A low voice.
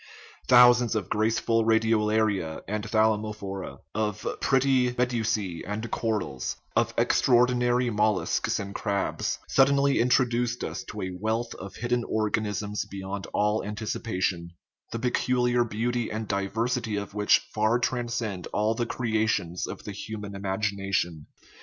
Yes: low, 110 Hz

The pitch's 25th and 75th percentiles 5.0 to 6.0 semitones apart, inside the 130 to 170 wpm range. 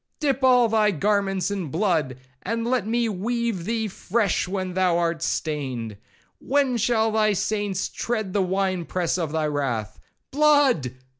Yes: average, 5.3 semitones; average, 140 wpm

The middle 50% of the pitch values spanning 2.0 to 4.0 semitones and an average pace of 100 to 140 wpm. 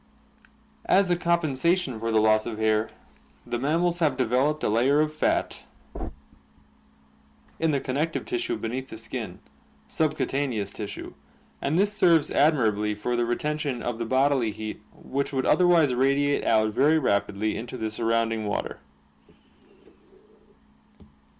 No: wide, 5.5 semitones; slow, 135 wpm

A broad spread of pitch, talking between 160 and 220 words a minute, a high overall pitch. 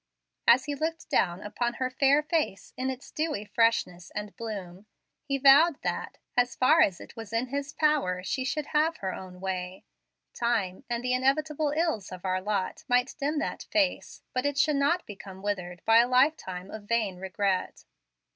Yes: wide, 6.7 semitones; average, 180 wpm; high, 240 Hz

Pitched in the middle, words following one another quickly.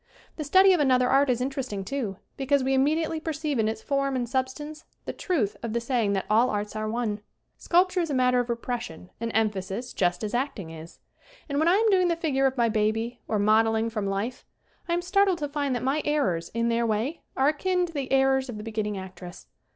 No: very high, 250 Hz; fast, 230 wpm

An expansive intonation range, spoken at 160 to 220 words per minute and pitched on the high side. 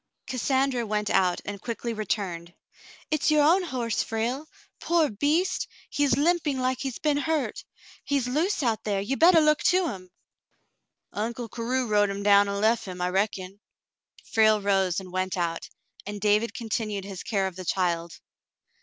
Yes: wide, 5.7 semitones; average, 170 wpm; high, 220 Hz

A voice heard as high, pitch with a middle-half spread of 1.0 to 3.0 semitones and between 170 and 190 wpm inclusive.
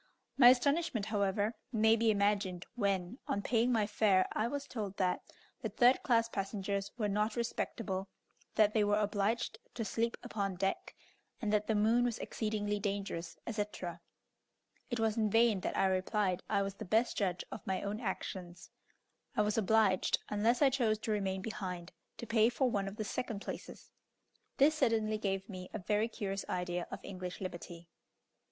Yes: high, 210 Hz; narrow, 2.6 semitones; average, 175 wpm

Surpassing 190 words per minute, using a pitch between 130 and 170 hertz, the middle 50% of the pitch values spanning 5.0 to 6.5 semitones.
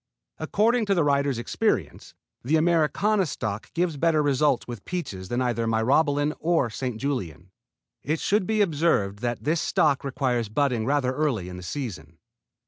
No: average, 155 wpm; medium, 140 Hz; wide, 5.6 semitones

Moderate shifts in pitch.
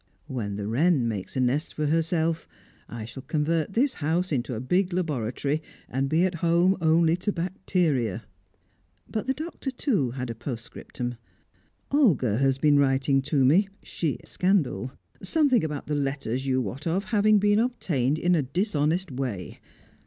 No: wide, 5.7 semitones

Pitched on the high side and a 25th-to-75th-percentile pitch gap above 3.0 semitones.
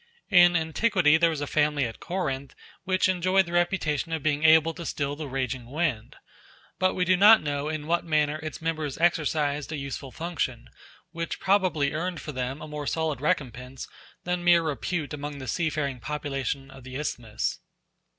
No: medium, 155 Hz; average, 3.5 semitones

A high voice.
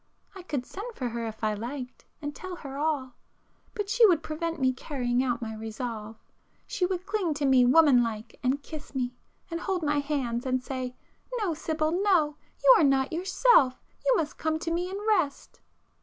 Yes: very high, 290 Hz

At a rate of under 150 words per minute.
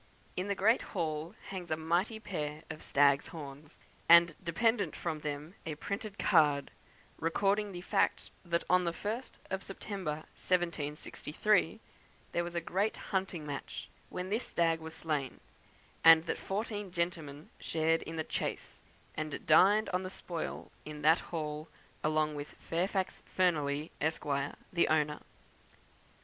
Yes: average, 140 wpm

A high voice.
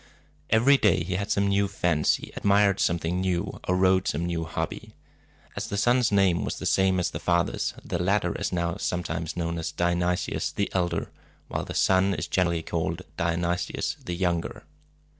No: very low, 90 Hz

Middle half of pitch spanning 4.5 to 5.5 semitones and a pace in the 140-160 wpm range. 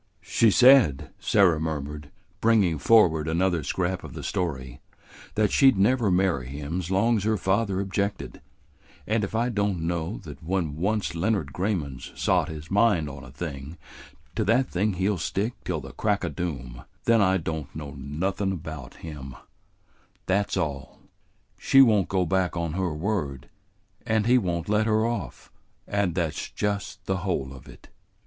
No: average, 5.1 semitones; average, 170 wpm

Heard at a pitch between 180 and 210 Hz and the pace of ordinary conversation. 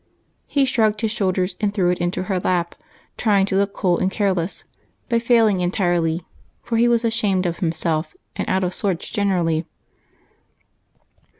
Yes: high, 190 Hz; average, 160 wpm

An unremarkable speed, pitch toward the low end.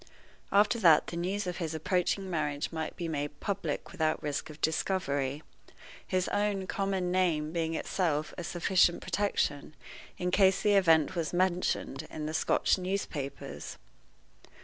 No: average, 150 wpm; medium, 175 Hz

